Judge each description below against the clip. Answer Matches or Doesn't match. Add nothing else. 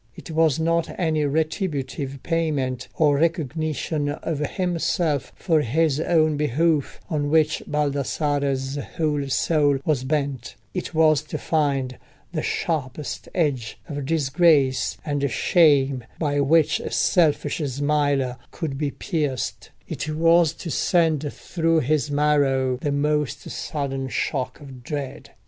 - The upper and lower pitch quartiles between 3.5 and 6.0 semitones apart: Doesn't match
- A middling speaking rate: Doesn't match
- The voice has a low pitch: Doesn't match